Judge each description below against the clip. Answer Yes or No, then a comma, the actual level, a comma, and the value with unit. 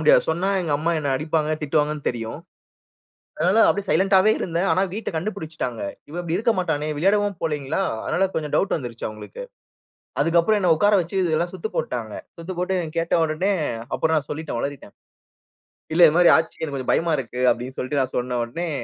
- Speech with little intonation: No, average, 4.1 semitones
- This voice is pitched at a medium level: Yes, medium, 160 Hz